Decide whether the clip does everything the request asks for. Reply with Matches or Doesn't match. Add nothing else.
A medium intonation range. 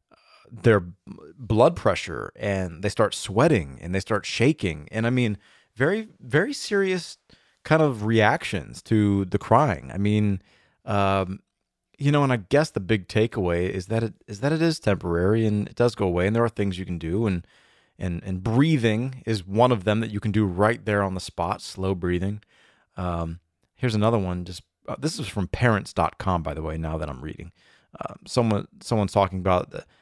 Matches